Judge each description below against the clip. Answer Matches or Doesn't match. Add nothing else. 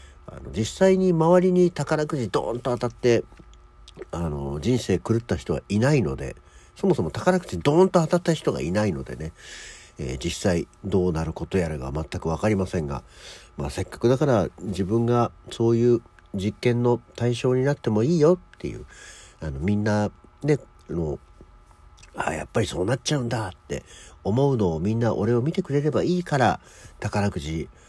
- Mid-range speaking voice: Doesn't match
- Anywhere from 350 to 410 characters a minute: Doesn't match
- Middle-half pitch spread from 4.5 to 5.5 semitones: Doesn't match